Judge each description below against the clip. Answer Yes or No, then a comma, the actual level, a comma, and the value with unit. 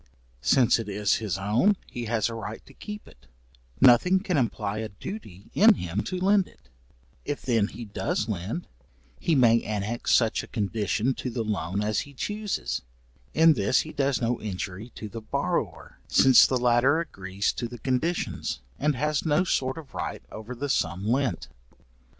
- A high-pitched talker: No, low, 120 Hz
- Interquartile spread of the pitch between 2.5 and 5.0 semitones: No, wide, 5.4 semitones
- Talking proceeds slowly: No, average, 175 wpm